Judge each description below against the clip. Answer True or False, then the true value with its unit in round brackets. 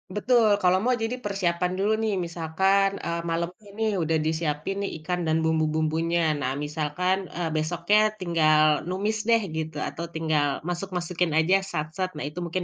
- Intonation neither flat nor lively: True (3.4 semitones)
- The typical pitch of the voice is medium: True (170 Hz)